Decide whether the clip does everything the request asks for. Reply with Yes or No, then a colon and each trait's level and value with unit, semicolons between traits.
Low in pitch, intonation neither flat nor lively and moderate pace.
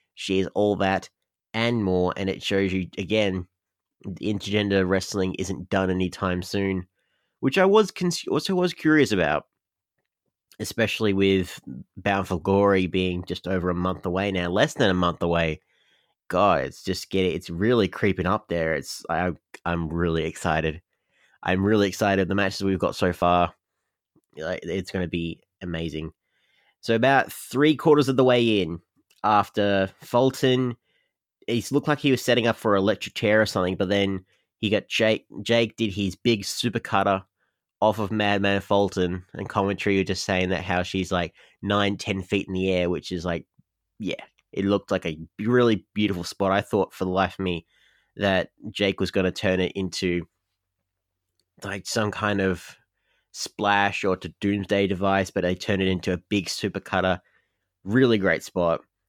No: very low, 95 Hz; narrow, 2.3 semitones; average, 175 wpm